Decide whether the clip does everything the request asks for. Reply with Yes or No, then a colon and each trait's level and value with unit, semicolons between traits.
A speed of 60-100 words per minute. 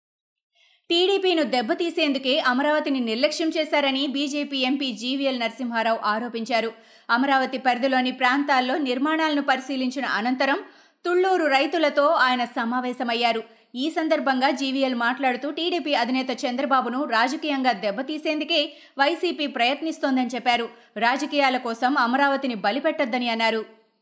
Yes: average, 90 wpm